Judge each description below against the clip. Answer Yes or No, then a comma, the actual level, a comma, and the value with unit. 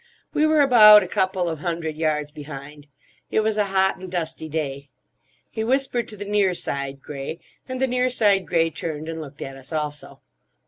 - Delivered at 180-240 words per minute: Yes, average, 190 wpm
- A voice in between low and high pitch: Yes, medium, 170 Hz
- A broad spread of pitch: Yes, wide, 5.9 semitones